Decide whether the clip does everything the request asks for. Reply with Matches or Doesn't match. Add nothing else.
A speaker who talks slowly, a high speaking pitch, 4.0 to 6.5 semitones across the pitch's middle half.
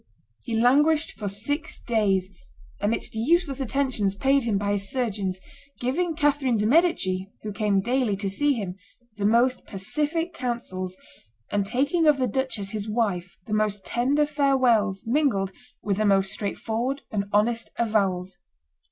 Doesn't match